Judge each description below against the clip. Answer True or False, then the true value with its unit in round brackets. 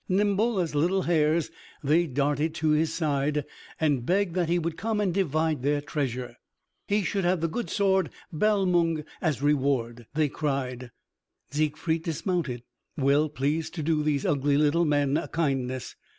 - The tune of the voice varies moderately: True (3.4 semitones)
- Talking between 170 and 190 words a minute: False (155 wpm)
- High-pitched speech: False (155 Hz)